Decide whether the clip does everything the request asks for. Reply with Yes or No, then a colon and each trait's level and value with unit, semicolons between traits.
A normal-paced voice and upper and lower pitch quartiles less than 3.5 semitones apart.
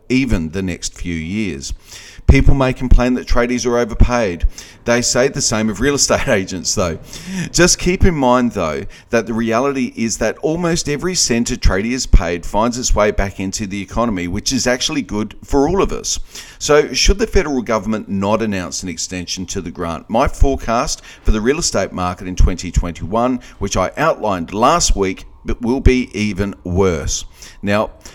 No: average, 180 wpm; average, 5.0 semitones